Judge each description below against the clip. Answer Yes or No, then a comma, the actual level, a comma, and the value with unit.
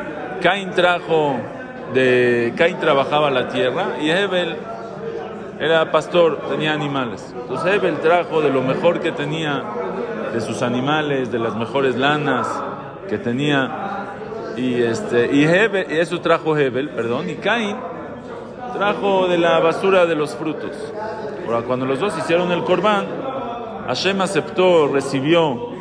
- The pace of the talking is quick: No, average, 130 wpm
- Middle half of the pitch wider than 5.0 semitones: Yes, wide, 5.5 semitones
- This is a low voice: No, medium, 155 Hz